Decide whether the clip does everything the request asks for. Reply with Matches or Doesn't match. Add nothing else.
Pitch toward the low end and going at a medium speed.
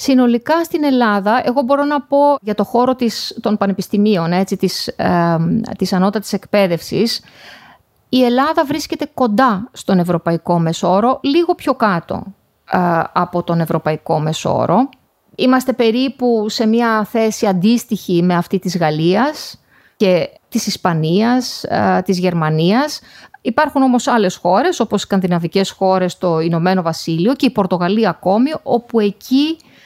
Doesn't match